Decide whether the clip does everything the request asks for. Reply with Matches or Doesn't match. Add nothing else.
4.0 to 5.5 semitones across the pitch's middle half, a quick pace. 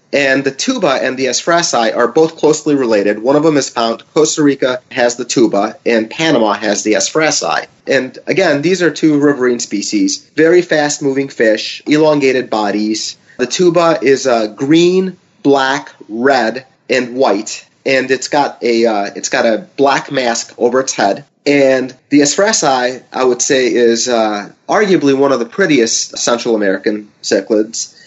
Doesn't match